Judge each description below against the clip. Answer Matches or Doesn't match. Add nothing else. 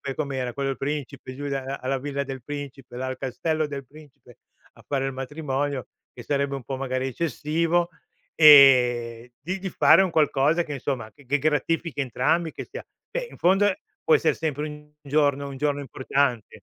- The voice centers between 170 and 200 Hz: Doesn't match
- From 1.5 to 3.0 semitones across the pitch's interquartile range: Matches